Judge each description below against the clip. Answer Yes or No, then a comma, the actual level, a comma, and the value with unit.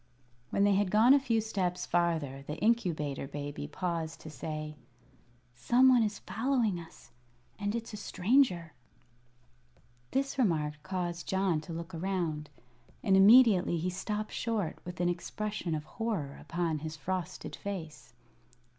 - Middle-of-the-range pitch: Yes, medium, 180 Hz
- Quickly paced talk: No, average, 140 wpm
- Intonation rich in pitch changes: No, average, 5.0 semitones